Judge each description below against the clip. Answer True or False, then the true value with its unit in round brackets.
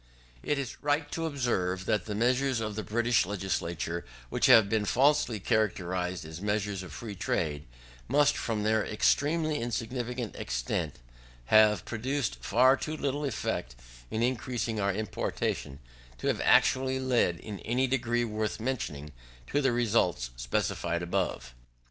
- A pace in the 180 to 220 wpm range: False (140 wpm)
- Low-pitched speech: True (110 Hz)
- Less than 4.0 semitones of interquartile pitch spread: False (5.6 semitones)